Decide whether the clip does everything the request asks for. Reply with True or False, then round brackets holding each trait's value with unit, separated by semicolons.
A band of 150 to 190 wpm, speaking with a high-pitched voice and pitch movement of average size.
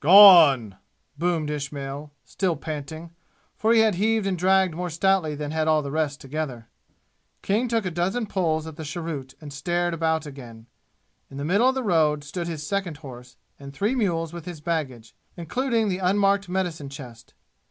False (175 wpm; 160 Hz; 4.6 semitones)